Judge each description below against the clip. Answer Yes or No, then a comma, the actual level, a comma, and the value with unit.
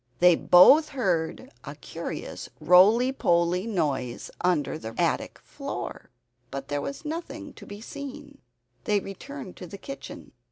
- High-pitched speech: Yes, high, 195 Hz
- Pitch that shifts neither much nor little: No, wide, 8.2 semitones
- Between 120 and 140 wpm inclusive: Yes, slow, 135 wpm